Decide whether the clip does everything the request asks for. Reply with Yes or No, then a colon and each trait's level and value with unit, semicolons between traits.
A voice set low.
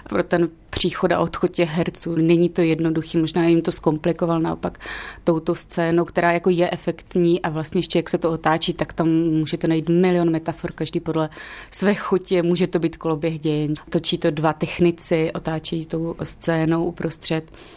No: medium, 170 Hz